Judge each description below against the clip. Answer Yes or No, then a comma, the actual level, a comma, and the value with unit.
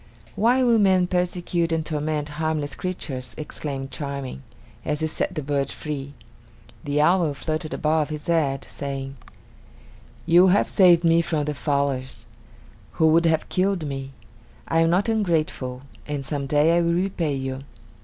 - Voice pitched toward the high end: No, medium, 155 Hz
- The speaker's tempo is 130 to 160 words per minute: Yes, average, 155 wpm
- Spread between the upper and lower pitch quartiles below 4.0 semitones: Yes, average, 3.4 semitones